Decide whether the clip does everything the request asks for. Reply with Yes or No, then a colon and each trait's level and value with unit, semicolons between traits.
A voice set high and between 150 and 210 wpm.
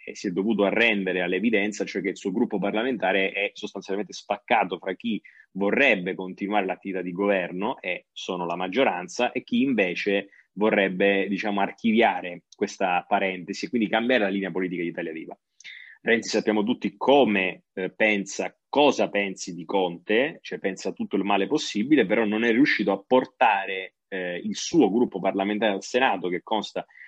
No: low, 100 Hz; average, 165 wpm